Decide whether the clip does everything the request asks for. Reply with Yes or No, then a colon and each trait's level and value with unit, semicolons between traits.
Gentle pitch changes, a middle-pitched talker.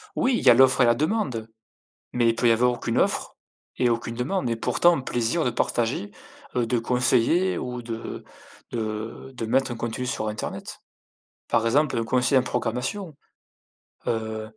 No: narrow, 2.3 semitones; low, 120 Hz